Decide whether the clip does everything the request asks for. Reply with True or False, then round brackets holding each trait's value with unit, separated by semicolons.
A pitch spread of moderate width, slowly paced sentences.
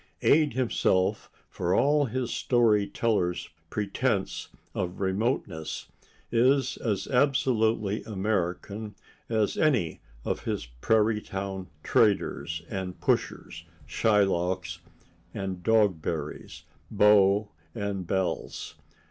True (3.4 semitones; 90 wpm)